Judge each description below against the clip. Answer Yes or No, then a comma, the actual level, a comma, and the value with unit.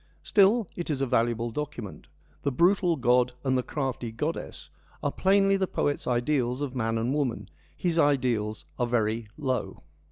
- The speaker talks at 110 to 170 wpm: Yes, average, 165 wpm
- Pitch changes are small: No, average, 4.7 semitones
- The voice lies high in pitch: No, low, 130 Hz